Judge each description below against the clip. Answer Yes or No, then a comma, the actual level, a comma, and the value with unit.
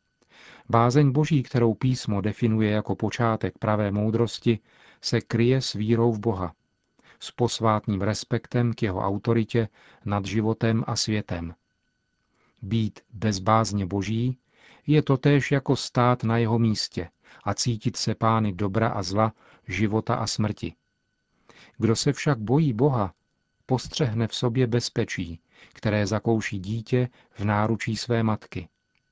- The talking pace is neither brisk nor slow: Yes, average, 125 wpm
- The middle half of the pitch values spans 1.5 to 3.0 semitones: Yes, narrow, 2.4 semitones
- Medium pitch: No, low, 115 Hz